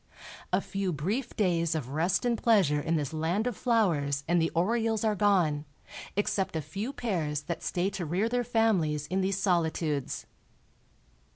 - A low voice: No, medium, 180 Hz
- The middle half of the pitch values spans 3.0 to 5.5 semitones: Yes, average, 5.2 semitones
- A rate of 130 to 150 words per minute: No, average, 165 wpm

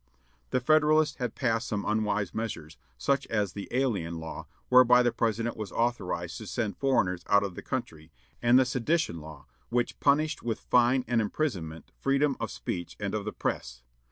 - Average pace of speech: Yes, average, 175 wpm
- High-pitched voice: No, low, 115 Hz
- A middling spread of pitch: Yes, average, 5.0 semitones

